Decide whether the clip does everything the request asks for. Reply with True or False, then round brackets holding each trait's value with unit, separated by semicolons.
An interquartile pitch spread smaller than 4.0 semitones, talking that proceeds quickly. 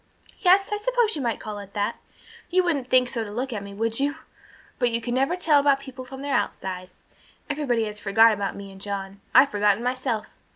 False (5.4 semitones; 215 wpm)